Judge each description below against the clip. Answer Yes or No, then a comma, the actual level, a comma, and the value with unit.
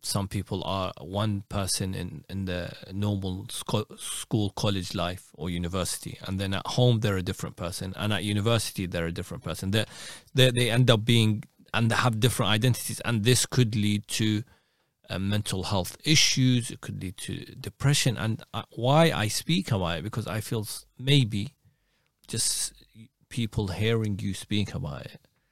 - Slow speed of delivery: No, average, 170 wpm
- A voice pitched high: No, low, 105 Hz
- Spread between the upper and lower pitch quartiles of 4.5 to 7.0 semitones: No, average, 3.8 semitones